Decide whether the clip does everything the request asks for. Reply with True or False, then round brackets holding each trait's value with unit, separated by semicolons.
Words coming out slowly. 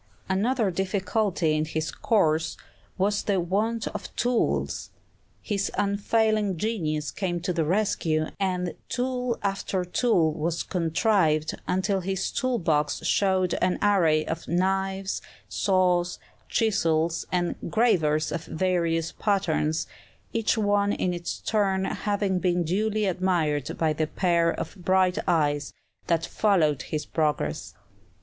True (125 wpm)